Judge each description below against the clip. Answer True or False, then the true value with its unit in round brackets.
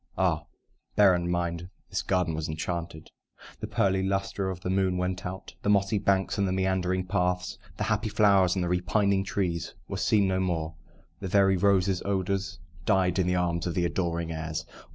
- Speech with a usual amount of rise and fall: False (1.9 semitones)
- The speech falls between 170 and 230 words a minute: True (185 wpm)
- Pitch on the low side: True (95 Hz)